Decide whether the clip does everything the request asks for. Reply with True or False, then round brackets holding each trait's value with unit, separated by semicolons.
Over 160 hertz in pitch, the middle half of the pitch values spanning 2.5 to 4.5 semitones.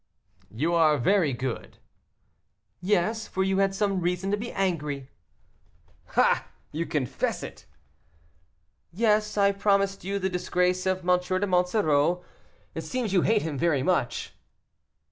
True (185 Hz; 3.1 semitones)